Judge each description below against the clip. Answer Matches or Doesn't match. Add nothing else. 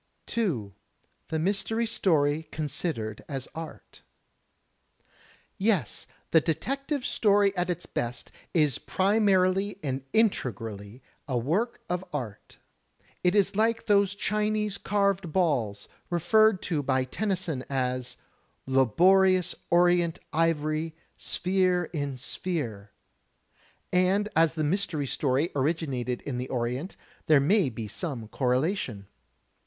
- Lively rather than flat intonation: Matches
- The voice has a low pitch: Doesn't match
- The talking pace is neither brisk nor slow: Doesn't match